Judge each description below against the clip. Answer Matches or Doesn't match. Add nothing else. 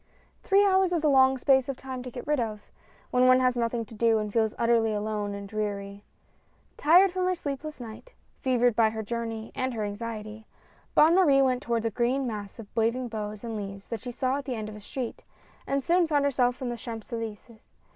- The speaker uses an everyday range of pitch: Matches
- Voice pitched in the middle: Doesn't match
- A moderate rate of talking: Doesn't match